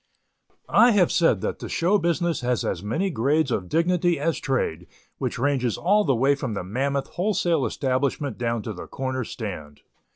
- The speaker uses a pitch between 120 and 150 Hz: Yes, medium, 140 Hz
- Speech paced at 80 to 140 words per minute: No, average, 175 wpm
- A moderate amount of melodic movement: No, wide, 5.9 semitones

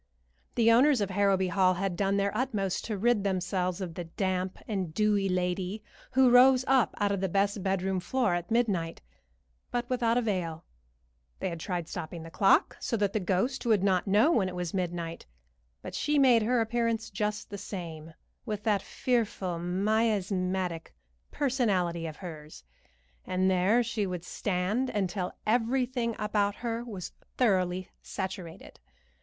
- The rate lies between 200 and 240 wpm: No, average, 155 wpm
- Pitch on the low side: No, high, 195 Hz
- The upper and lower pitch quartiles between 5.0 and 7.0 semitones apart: No, average, 3.9 semitones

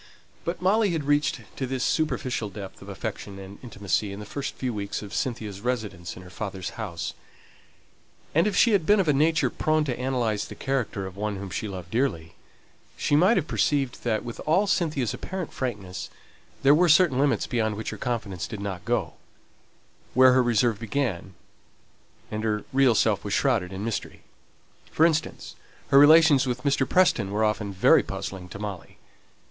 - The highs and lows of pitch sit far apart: Yes, wide, 6.3 semitones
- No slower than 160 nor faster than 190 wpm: Yes, average, 180 wpm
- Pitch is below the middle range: Yes, low, 120 Hz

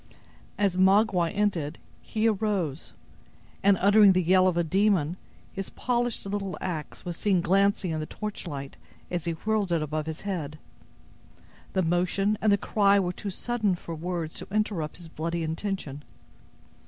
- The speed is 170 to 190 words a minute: No, average, 155 wpm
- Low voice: No, medium, 185 Hz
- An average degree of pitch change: Yes, average, 3.6 semitones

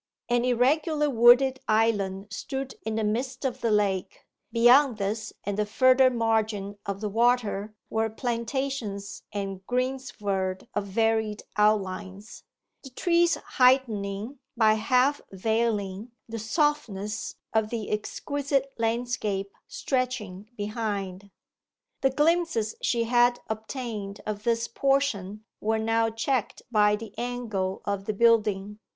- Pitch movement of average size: Yes, average, 3.4 semitones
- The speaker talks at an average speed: No, slow, 120 wpm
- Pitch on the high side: Yes, high, 225 Hz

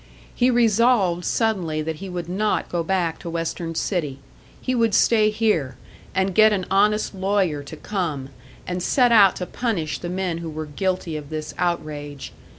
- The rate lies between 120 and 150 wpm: No, average, 170 wpm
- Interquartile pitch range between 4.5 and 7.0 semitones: Yes, average, 4.8 semitones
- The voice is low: No, medium, 180 Hz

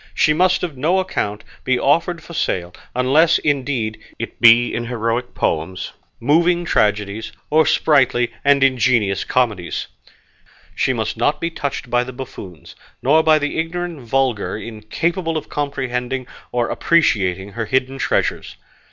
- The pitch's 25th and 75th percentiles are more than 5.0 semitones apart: Yes, wide, 5.5 semitones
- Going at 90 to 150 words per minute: Yes, average, 140 wpm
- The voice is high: No, low, 130 Hz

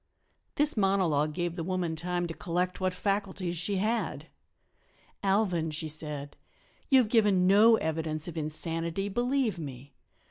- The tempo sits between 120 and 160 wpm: Yes, average, 140 wpm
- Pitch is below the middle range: No, medium, 180 Hz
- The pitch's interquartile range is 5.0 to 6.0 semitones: No, average, 3.8 semitones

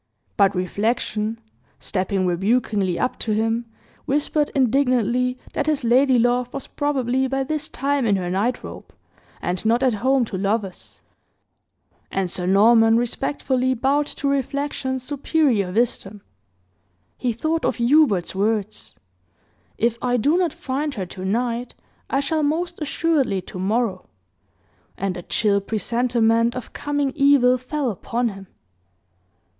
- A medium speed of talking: No, slow, 130 wpm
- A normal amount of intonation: Yes, average, 4.7 semitones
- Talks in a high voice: Yes, high, 240 Hz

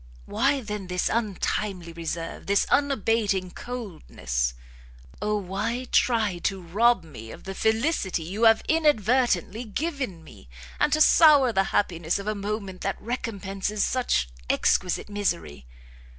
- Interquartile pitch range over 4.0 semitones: Yes, average, 4.5 semitones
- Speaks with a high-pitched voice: Yes, high, 205 Hz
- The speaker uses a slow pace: Yes, slow, 130 wpm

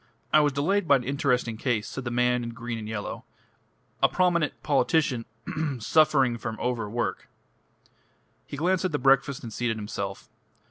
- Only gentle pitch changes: No, average, 4.1 semitones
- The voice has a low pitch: Yes, low, 125 Hz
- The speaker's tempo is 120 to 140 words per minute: No, average, 165 wpm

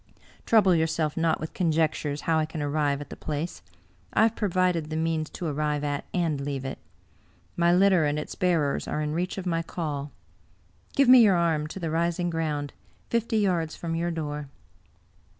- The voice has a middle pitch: Yes, medium, 160 Hz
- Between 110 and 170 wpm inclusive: No, average, 185 wpm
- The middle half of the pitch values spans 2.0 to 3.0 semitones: Yes, average, 2.7 semitones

